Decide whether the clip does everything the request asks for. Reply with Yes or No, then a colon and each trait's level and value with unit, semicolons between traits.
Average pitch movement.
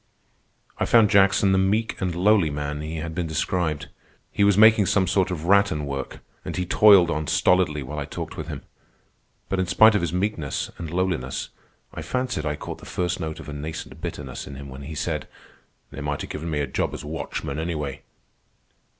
Yes: average, 4.4 semitones